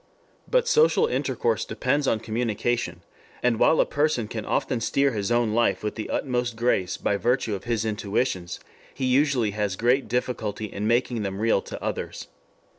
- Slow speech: No, average, 170 wpm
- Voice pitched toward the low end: Yes, low, 115 Hz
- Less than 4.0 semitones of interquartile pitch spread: Yes, average, 3.3 semitones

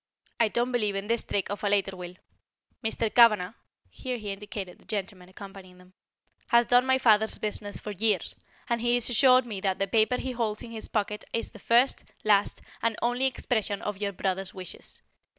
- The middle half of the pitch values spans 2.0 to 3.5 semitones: Yes, average, 3.2 semitones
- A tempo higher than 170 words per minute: Yes, average, 190 wpm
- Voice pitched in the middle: No, high, 210 Hz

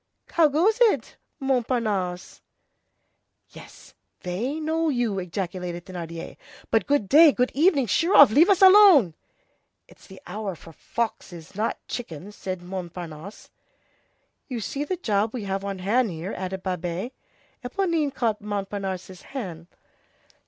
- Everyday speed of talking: No, slow, 130 wpm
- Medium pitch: No, high, 210 Hz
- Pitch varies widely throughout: Yes, wide, 7.1 semitones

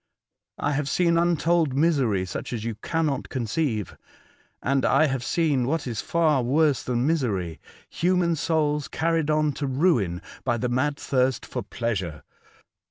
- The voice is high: No, medium, 140 Hz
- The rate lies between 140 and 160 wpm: Yes, average, 150 wpm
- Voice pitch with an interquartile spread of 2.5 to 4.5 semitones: No, average, 5.0 semitones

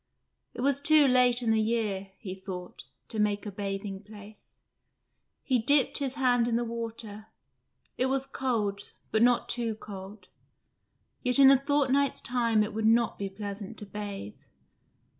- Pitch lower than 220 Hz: No, high, 225 Hz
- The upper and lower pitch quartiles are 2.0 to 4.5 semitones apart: Yes, average, 3.6 semitones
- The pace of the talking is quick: No, average, 160 wpm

